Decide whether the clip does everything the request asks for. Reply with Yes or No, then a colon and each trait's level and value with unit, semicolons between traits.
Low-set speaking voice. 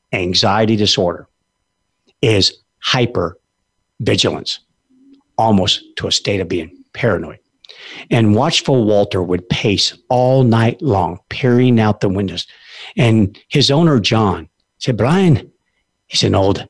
Yes: low, 115 Hz